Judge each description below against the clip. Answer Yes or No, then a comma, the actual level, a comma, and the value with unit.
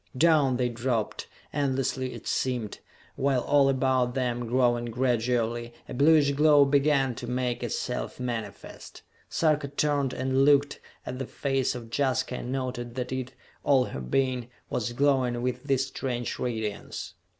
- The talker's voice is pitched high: No, low, 130 Hz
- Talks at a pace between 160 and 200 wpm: No, average, 145 wpm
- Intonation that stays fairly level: Yes, narrow, 2.1 semitones